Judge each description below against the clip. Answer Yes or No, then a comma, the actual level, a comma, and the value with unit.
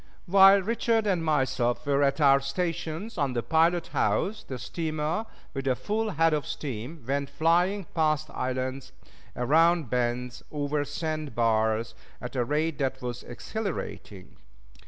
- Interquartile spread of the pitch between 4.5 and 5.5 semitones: Yes, average, 4.8 semitones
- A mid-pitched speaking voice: Yes, medium, 150 Hz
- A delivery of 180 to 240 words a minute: No, average, 140 wpm